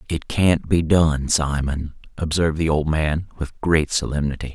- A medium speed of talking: Yes, average, 160 wpm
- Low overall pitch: Yes, very low, 80 Hz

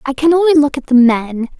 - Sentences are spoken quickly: Yes, fast, 265 wpm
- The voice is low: No, very high, 280 Hz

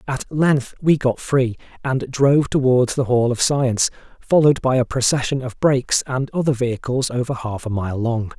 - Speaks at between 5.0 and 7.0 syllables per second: Yes, 5.1 syllables/s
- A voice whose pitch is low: Yes, low, 130 Hz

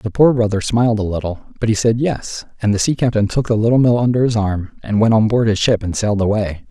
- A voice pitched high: No, low, 110 Hz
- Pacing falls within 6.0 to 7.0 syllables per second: Yes, 6.2 syllables/s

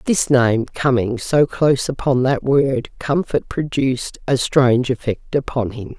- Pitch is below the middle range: Yes, low, 130 Hz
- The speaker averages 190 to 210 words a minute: No, average, 150 wpm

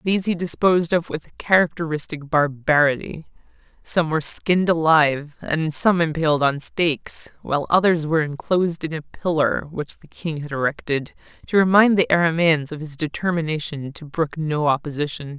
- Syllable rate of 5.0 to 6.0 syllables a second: Yes, 5.2 syllables/s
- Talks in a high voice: No, medium, 160 Hz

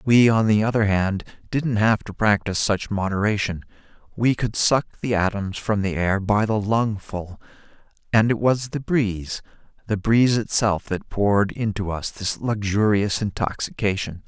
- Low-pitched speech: Yes, low, 105 Hz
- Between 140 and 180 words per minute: Yes, average, 155 wpm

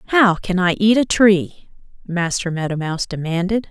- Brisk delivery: No, average, 160 wpm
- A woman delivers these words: Yes, female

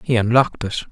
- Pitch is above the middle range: No, low, 115 Hz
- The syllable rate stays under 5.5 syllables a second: No, 6.4 syllables/s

